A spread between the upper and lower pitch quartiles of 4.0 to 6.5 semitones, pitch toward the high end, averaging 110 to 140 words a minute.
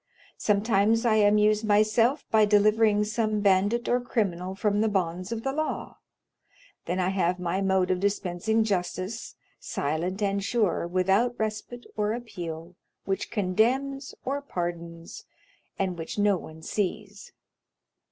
No: average, 3.1 semitones; high, 205 Hz; slow, 135 wpm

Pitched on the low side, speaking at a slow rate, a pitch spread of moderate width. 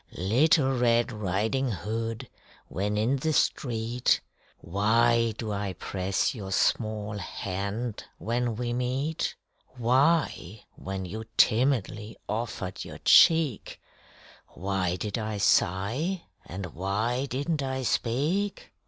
Yes: low, 115 Hz; slow, 110 wpm; average, 4.2 semitones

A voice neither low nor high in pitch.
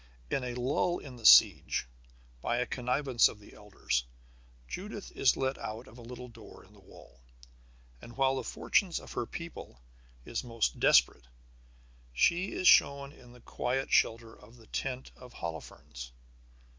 No: low, 125 Hz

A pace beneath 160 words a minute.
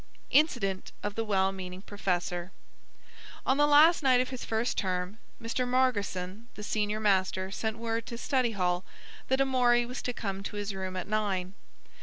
No: average, 170 wpm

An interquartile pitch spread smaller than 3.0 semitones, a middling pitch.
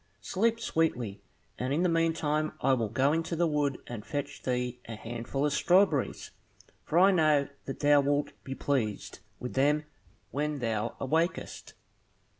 No: average, 4.3 semitones; medium, 145 Hz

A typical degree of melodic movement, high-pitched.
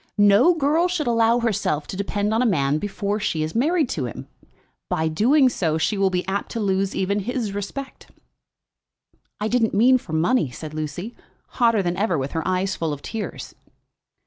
No: wide, 5.9 semitones; high, 200 Hz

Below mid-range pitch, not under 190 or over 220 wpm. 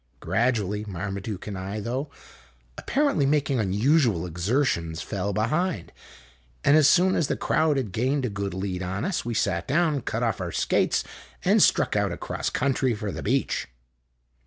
No: low, 110 Hz; average, 165 wpm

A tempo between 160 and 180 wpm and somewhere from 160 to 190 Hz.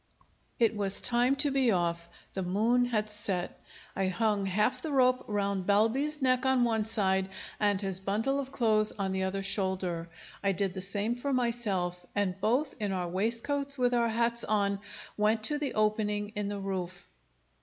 No: average, 175 wpm; high, 210 Hz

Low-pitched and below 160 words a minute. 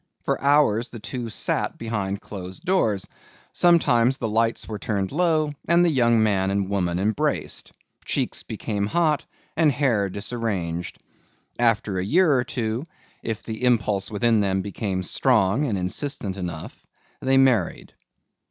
Yes: low, 110 Hz; average, 145 wpm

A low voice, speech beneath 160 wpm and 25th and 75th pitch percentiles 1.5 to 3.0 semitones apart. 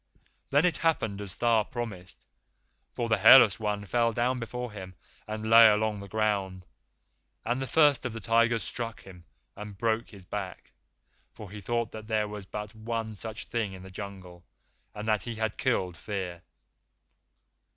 No: low, 110 Hz; average, 170 wpm; average, 2.7 semitones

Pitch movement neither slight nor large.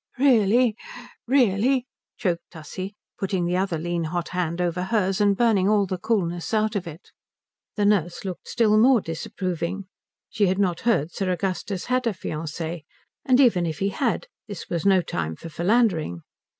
Yes: average, 3.9 semitones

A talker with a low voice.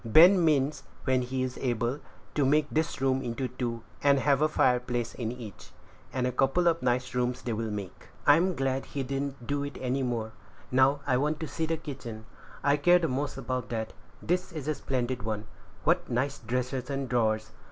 Yes: low, 130 Hz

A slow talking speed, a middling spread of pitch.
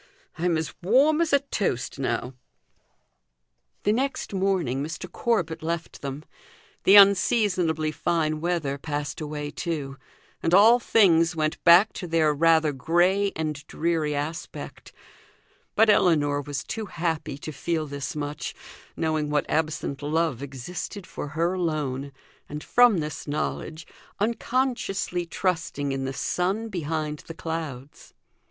Yes: slow, 130 wpm; average, 3.8 semitones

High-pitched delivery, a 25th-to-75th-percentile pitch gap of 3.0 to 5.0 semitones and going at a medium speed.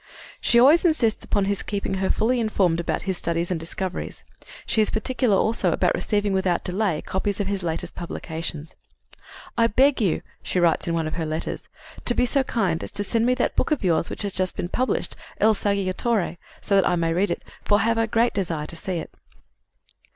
No: high, 195 Hz; average, 4.6 semitones; fast, 215 wpm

